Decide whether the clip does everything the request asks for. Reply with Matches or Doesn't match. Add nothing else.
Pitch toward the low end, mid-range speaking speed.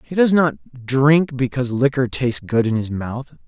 Matches